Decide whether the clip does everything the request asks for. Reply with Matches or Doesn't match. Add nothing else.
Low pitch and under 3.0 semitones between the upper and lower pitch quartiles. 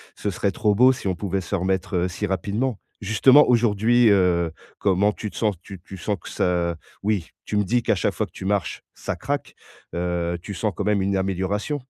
Matches